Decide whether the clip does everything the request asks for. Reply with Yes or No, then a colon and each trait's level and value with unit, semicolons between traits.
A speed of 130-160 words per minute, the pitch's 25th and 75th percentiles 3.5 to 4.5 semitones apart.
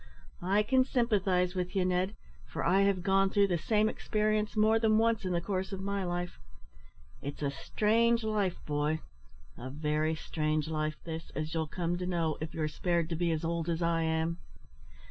No: average, 190 wpm; average, 4.0 semitones